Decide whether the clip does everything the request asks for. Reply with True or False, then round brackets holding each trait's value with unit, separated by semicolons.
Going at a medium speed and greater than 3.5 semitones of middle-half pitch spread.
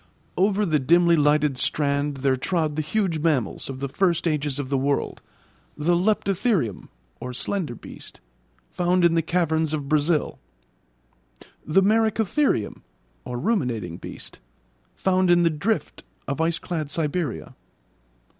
False (125 wpm; 4.1 semitones)